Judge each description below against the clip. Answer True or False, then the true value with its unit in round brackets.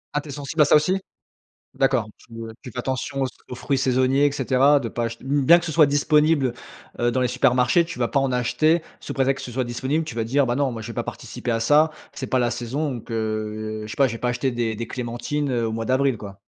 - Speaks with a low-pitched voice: True (130 Hz)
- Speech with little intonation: False (3.2 semitones)